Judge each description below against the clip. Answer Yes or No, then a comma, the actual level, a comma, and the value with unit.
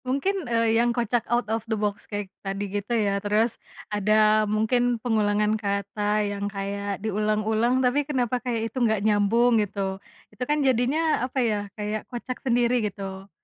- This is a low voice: No, high, 215 Hz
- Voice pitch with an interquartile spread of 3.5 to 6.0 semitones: No, average, 2.8 semitones